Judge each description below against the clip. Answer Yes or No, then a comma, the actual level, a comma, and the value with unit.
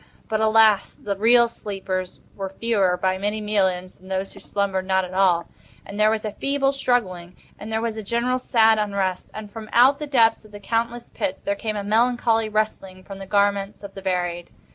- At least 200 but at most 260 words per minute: Yes, fast, 205 wpm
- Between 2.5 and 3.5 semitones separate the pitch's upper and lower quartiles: Yes, average, 2.8 semitones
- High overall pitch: Yes, high, 205 Hz